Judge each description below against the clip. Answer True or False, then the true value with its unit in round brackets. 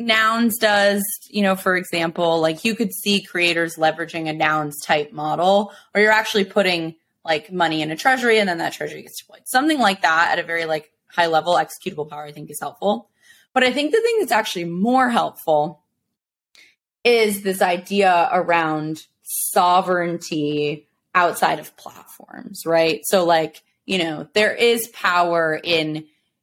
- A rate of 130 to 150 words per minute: False (165 wpm)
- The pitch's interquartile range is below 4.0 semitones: False (5.0 semitones)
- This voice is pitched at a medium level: True (180 Hz)